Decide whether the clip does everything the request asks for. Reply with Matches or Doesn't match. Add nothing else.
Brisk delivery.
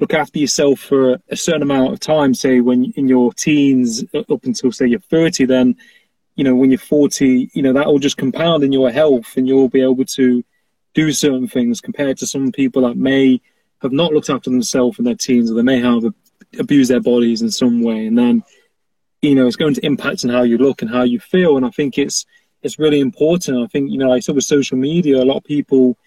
Matches